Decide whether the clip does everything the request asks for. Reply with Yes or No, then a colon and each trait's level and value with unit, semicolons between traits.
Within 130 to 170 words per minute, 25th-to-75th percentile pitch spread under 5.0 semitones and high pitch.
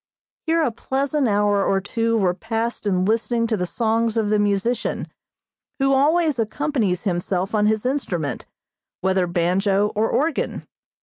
Yes: average, 145 wpm; average, 3.9 semitones; high, 220 Hz